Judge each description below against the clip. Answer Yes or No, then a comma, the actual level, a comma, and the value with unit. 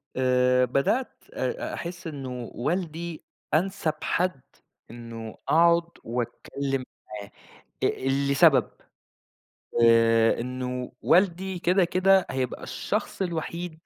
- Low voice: No, medium, 145 Hz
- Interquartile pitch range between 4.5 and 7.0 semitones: Yes, wide, 5.6 semitones